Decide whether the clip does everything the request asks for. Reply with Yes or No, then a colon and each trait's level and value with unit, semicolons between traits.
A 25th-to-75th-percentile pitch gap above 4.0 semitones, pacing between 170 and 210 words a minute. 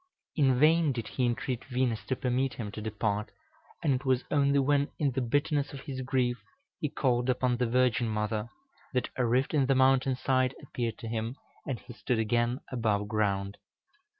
No: narrow, 2.6 semitones; average, 185 wpm